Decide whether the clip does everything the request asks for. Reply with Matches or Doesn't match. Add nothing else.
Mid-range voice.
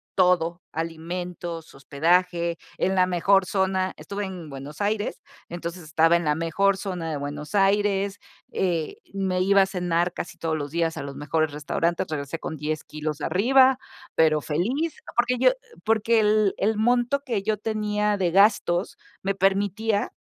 Matches